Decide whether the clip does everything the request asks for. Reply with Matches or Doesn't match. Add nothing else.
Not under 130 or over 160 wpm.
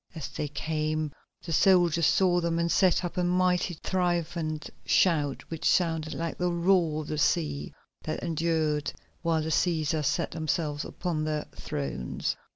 Matches